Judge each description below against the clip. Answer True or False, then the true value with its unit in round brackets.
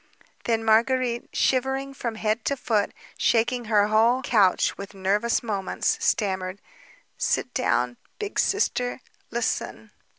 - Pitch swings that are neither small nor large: True (3.5 semitones)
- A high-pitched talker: True (230 Hz)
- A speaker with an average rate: False (120 wpm)